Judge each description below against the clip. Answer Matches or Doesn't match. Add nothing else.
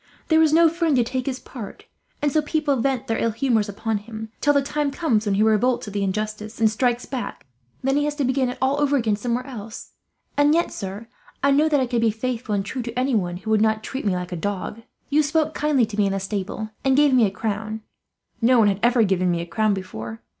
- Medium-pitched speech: Doesn't match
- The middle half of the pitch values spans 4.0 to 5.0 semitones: Matches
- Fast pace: Matches